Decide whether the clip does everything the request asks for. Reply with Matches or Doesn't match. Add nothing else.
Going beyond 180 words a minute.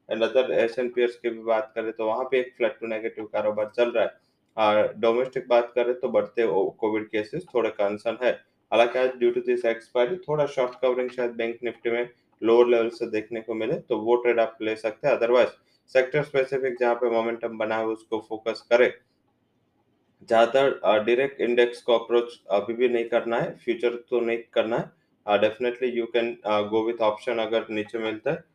Matches